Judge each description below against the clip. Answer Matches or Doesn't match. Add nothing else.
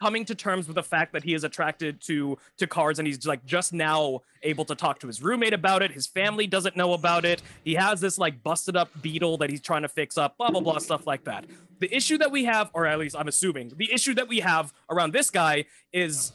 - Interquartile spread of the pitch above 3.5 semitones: Matches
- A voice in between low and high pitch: Matches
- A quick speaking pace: Matches